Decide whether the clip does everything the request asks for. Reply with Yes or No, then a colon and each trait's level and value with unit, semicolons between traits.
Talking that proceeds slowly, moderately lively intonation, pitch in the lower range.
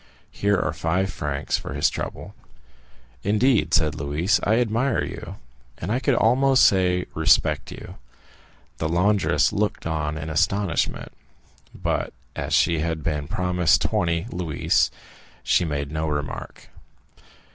Yes: slow, 130 wpm; average, 4.9 semitones; very low, 85 Hz